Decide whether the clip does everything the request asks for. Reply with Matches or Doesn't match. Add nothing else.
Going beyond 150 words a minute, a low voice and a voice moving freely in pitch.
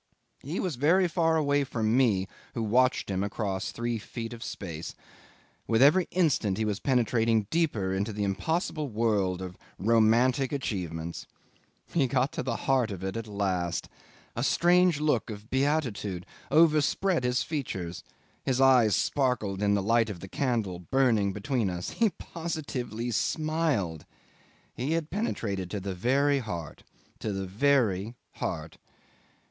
Doesn't match